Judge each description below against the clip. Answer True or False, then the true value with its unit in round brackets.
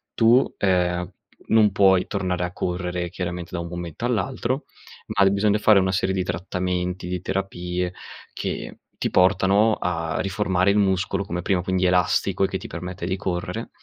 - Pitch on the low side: True (95 Hz)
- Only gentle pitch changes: True (1.8 semitones)